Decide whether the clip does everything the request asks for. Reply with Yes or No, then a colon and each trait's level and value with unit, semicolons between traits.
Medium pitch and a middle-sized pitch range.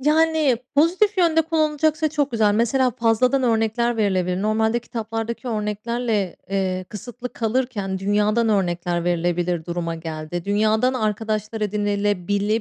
No: high, 220 Hz; average, 4.2 semitones